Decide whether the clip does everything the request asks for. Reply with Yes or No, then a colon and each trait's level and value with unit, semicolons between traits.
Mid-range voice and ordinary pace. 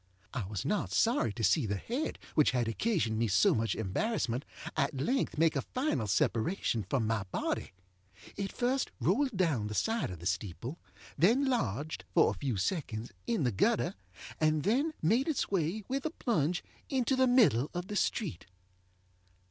Yes: medium, 155 Hz; average, 170 wpm